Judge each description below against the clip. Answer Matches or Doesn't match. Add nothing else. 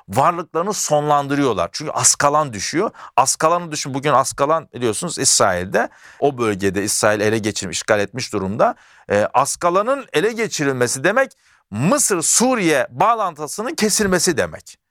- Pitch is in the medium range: Matches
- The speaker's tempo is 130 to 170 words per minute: Doesn't match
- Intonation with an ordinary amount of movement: Doesn't match